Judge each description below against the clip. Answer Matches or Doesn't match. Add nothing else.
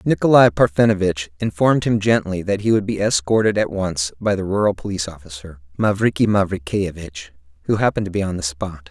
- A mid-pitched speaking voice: Doesn't match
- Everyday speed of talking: Matches